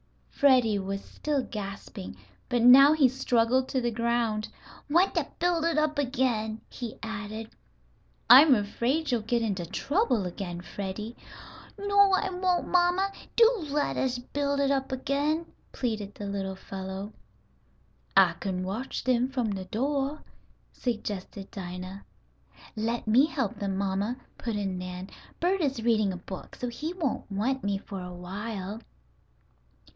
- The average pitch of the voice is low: No, high, 235 Hz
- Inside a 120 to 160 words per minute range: Yes, average, 145 wpm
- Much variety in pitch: Yes, wide, 6.0 semitones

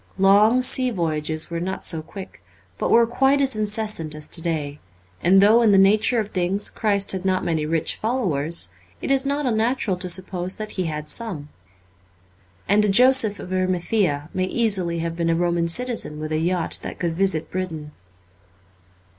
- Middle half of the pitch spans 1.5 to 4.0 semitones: No, average, 4.6 semitones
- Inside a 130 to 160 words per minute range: No, average, 180 wpm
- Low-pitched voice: No, medium, 185 Hz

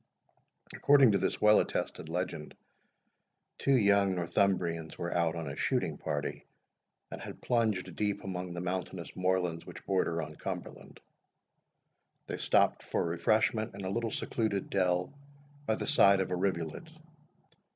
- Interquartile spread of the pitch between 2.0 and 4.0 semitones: Yes, average, 3.1 semitones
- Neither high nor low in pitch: No, very low, 95 Hz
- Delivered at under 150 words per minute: Yes, average, 140 wpm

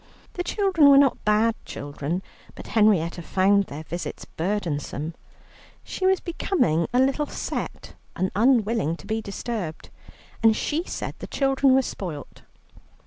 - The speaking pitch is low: No, high, 215 Hz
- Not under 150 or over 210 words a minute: No, average, 140 wpm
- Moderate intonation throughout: No, wide, 8.0 semitones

